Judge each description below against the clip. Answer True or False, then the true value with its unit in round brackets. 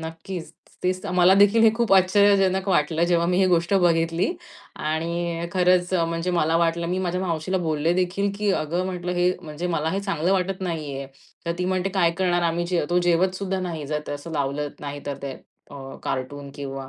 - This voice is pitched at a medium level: True (175 Hz)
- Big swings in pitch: False (2.5 semitones)